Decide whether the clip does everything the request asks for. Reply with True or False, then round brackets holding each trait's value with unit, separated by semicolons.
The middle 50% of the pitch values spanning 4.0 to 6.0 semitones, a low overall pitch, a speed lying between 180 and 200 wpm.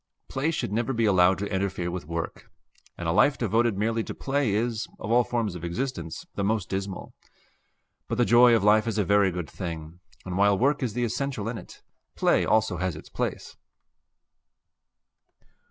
True (4.3 semitones; 105 Hz; 185 wpm)